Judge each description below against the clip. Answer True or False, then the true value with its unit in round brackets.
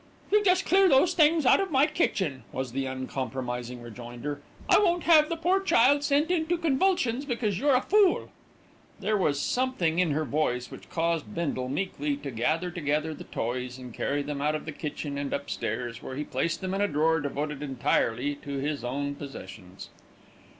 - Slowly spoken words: False (185 wpm)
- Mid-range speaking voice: True (150 Hz)